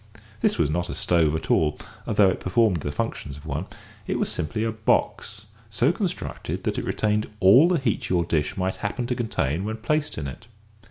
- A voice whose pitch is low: Yes, low, 100 Hz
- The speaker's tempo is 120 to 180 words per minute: No, fast, 205 wpm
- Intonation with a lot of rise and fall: Yes, wide, 5.9 semitones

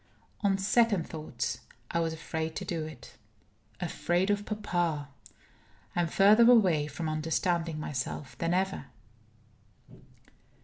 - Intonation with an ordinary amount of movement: Yes, average, 3.7 semitones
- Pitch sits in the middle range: Yes, medium, 170 Hz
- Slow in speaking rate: Yes, slow, 120 wpm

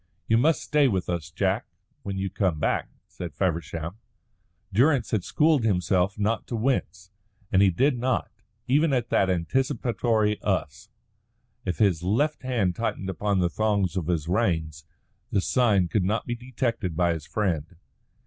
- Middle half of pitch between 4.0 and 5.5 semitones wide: Yes, average, 5.2 semitones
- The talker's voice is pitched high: No, low, 100 Hz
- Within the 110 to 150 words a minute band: No, average, 160 wpm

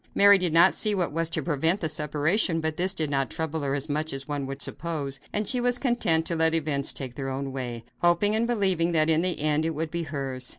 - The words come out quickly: Yes, fast, 250 wpm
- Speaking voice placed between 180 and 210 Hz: No, medium, 160 Hz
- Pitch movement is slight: No, average, 3.5 semitones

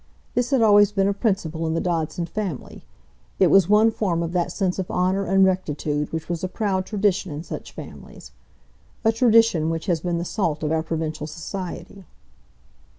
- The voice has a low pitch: No, medium, 180 Hz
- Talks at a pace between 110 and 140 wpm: No, average, 180 wpm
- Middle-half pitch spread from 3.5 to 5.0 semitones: Yes, average, 3.8 semitones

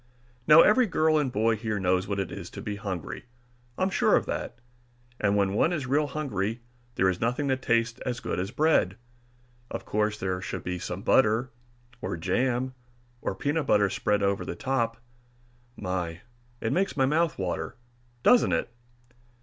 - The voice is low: Yes, low, 115 Hz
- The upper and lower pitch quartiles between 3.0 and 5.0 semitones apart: No, wide, 5.5 semitones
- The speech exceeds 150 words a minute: Yes, average, 175 wpm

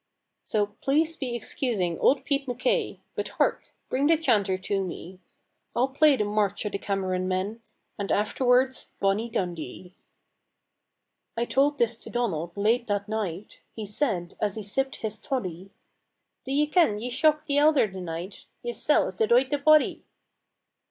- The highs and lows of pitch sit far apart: Yes, wide, 6.0 semitones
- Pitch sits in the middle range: No, high, 220 Hz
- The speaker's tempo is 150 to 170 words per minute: Yes, average, 160 wpm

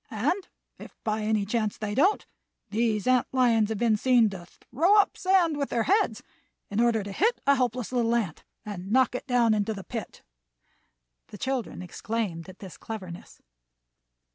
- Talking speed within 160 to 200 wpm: Yes, average, 170 wpm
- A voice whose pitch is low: No, high, 230 Hz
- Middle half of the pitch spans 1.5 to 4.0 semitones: Yes, average, 3.6 semitones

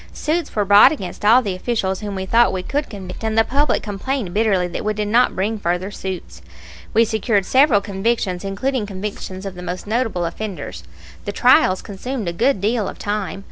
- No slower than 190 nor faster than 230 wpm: Yes, average, 195 wpm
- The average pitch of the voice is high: Yes, high, 205 Hz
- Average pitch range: Yes, average, 3.5 semitones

